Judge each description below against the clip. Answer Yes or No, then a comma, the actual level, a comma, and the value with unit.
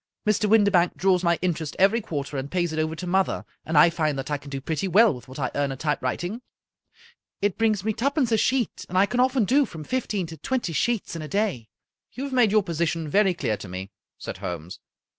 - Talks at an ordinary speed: No, fast, 235 wpm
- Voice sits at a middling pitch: Yes, medium, 180 Hz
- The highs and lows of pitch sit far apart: Yes, wide, 6.3 semitones